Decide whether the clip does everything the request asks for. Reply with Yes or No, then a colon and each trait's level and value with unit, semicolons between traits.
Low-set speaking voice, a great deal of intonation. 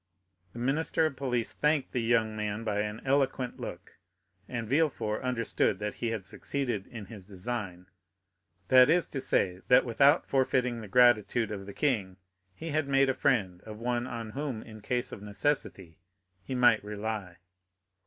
No: low, 115 Hz; average, 4.0 semitones